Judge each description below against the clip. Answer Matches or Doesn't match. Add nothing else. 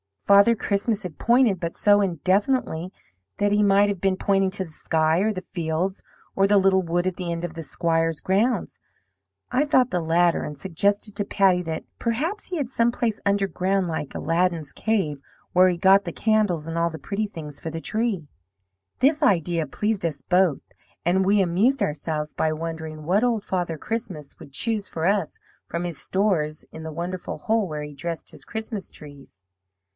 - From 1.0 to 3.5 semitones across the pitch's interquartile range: Doesn't match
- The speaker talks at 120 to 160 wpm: Doesn't match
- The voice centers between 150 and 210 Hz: Matches